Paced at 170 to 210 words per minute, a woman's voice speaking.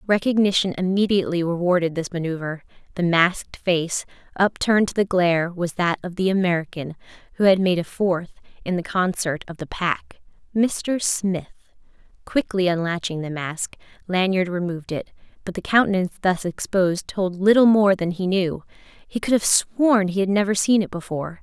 No: average, 160 wpm; female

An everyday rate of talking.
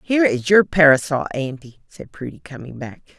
Yes: average, 170 wpm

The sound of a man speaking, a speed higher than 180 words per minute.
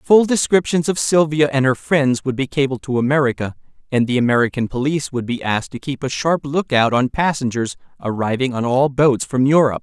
Yes: male; average, 200 wpm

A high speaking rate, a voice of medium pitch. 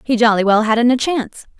No: fast, 225 wpm; high, 230 Hz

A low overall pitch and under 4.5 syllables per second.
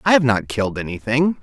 No: low, 120 Hz; 6.1 syllables/s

